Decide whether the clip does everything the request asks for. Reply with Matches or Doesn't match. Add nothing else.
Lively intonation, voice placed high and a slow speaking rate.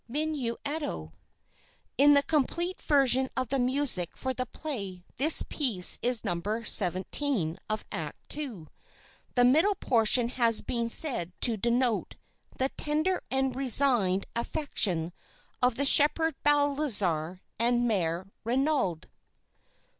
Matches